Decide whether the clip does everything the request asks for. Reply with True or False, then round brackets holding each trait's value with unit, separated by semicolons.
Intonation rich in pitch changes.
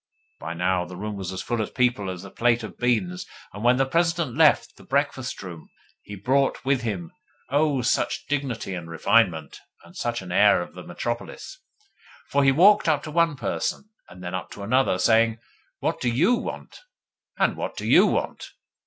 True (6.5 semitones)